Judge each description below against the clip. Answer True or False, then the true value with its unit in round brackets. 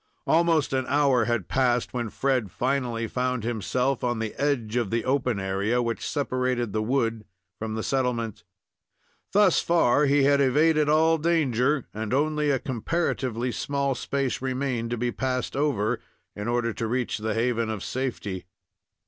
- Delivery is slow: False (155 wpm)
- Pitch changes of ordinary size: True (3.4 semitones)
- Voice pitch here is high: False (125 Hz)